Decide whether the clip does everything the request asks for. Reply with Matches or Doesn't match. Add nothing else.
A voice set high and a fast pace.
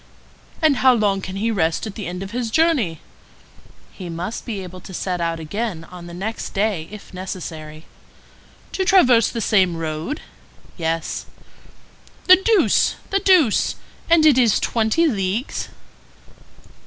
Doesn't match